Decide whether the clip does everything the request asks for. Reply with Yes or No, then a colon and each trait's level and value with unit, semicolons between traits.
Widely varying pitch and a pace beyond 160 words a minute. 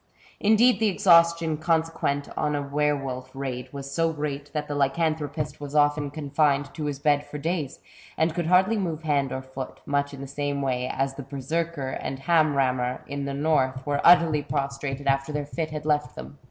No: narrow, 2.4 semitones; average, 195 wpm